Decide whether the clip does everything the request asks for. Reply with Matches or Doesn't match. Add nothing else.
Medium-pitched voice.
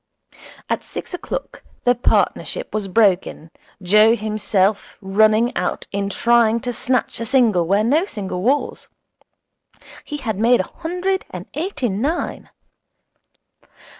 Doesn't match